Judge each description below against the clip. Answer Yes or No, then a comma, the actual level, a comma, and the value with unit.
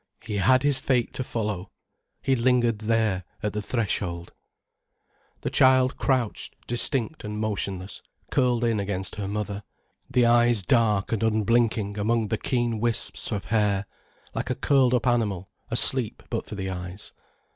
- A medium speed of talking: Yes, average, 150 wpm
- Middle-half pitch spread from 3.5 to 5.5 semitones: No, average, 2.9 semitones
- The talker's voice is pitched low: Yes, low, 110 Hz